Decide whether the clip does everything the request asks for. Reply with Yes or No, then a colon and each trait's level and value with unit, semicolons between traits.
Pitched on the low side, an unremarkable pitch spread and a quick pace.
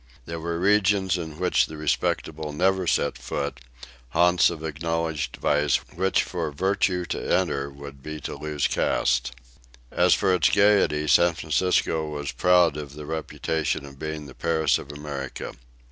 No: very low, 80 Hz; average, 3.2 semitones; average, 155 wpm